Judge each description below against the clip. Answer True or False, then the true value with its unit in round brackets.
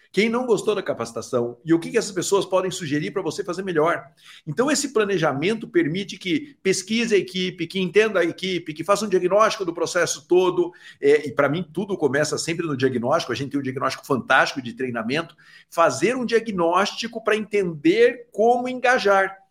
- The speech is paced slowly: False (185 wpm)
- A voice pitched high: True (195 Hz)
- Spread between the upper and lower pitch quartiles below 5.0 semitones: False (5.3 semitones)